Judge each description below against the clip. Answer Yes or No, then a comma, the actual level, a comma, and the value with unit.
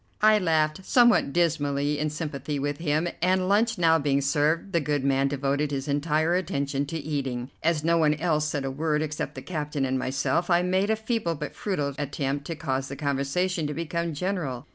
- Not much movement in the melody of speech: No, average, 3.2 semitones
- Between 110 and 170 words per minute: No, average, 195 wpm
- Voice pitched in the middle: Yes, medium, 150 Hz